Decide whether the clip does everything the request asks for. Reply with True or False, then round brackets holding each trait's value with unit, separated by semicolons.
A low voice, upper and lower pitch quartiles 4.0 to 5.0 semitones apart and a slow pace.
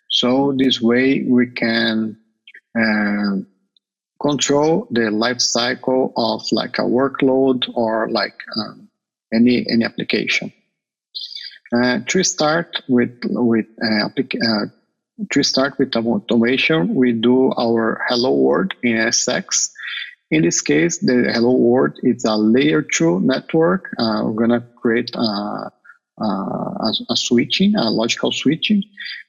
False (120 Hz; 3.2 semitones; 125 wpm)